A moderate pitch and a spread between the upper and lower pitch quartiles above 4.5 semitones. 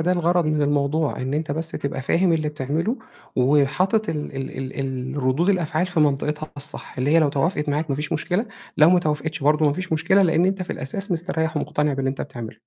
No: medium, 150 Hz; average, 3.3 semitones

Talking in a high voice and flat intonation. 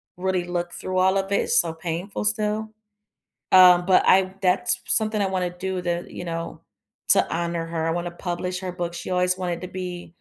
No: medium, 180 Hz; narrow, 1.4 semitones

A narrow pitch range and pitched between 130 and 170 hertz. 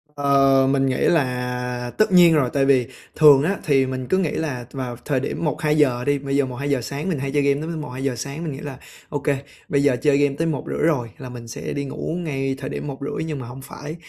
Yes: narrow, 2.2 semitones; medium, 140 Hz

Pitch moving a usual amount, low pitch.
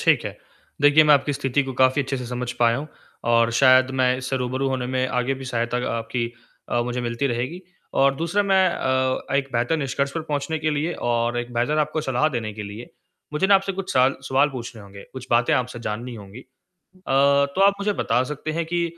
Yes: average, 3.5 semitones; low, 130 Hz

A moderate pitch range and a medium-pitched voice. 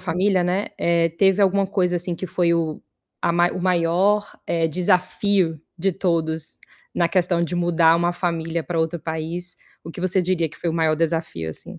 No: narrow, 1.9 semitones; medium, 170 Hz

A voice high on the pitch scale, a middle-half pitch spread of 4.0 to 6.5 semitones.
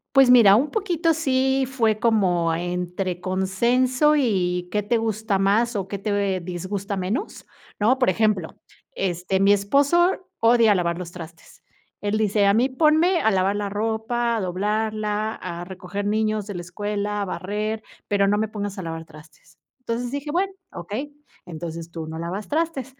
Yes: high, 205 Hz; average, 4.4 semitones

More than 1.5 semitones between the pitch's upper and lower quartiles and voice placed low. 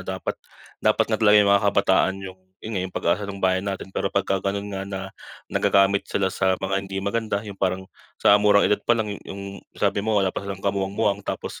No: narrow, 1.0 semitones; low, 100 Hz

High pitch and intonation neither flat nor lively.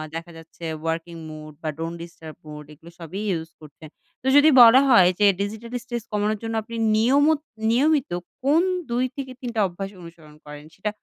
No: high, 195 Hz; wide, 6.6 semitones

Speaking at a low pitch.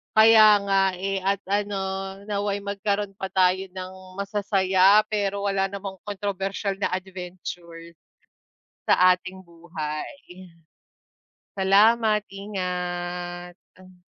No: high, 195 Hz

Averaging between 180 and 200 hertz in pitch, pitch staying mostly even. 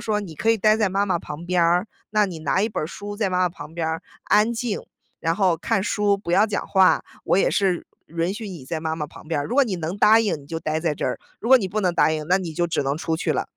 No: medium, 185 Hz; average, 4.1 semitones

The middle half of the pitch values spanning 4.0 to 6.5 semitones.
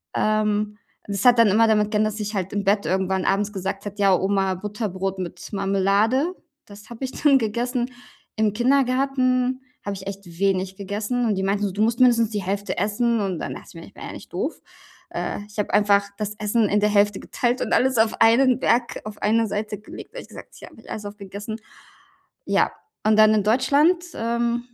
No: average, 2.9 semitones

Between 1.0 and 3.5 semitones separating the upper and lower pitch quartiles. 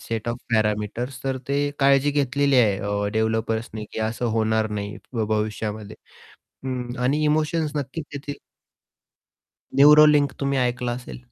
No: average, 4.3 semitones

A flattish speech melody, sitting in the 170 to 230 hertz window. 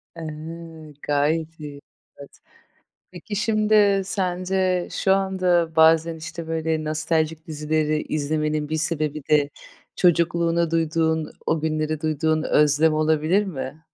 No: narrow, 2.0 semitones; medium, 160 Hz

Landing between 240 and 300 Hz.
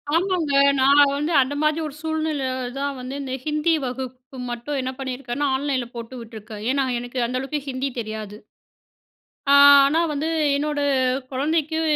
Yes: very high, 275 Hz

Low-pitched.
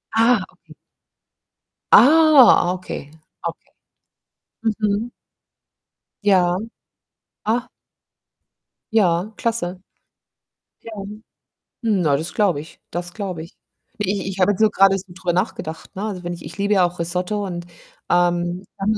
No: high, 190 Hz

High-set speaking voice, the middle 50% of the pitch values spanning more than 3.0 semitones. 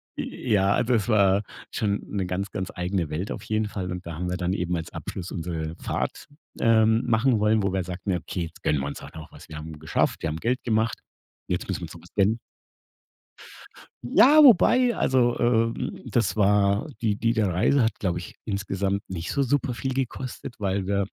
No: low, 100 Hz; average, 4.3 semitones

